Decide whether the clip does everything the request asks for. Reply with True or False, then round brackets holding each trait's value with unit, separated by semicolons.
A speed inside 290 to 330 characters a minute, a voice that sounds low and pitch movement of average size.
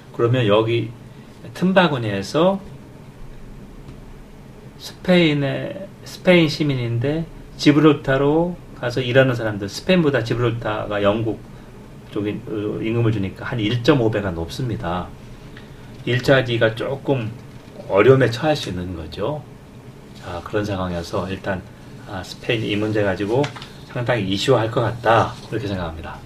False (265 characters per minute; 115 Hz; 4.9 semitones)